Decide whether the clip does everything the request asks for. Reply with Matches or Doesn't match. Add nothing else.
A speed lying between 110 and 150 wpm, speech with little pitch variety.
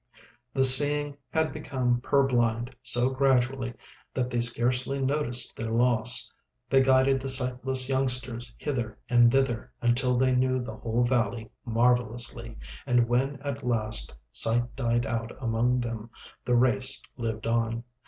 Matches